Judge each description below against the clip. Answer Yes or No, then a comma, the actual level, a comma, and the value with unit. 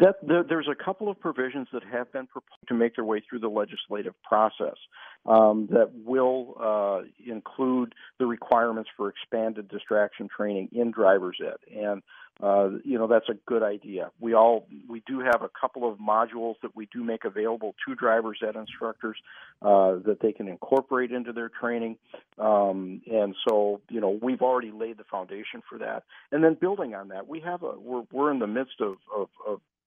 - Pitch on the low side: Yes, low, 115 Hz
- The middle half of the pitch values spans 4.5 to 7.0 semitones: No, average, 3.3 semitones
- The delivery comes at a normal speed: Yes, average, 190 wpm